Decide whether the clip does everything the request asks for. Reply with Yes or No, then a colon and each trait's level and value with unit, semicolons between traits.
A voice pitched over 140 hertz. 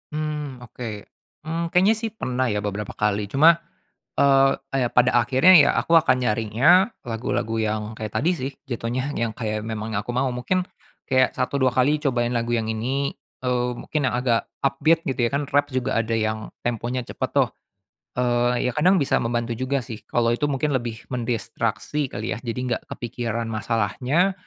No: low, 125 Hz